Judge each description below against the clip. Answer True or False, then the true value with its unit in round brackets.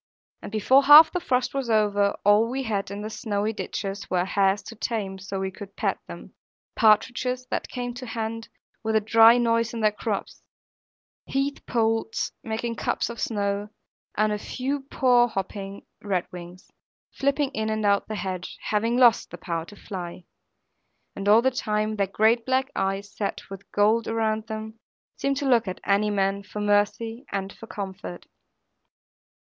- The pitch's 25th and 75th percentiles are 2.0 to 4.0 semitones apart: True (2.7 semitones)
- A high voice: True (215 Hz)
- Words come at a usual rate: True (170 wpm)